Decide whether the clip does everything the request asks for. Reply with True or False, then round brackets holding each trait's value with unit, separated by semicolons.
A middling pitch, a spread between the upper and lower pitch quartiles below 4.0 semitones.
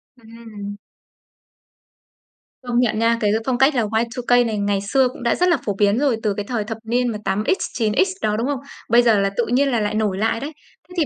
False (230 Hz; 2.9 semitones)